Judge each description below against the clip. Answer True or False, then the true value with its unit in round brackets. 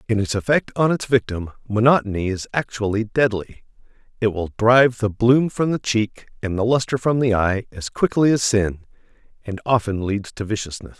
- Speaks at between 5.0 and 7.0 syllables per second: True (5.2 syllables/s)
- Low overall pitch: True (115 Hz)